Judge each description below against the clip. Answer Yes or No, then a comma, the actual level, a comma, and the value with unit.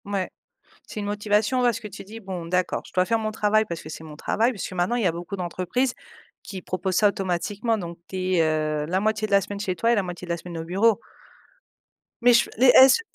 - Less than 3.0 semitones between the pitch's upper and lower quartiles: No, average, 3.7 semitones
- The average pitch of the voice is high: Yes, high, 200 Hz